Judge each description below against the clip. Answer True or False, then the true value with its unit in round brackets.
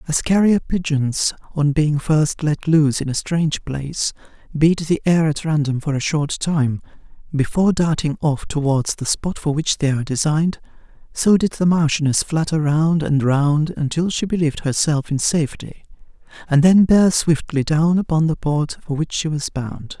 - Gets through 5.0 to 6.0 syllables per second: False (4.8 syllables/s)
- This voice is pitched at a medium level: True (155 Hz)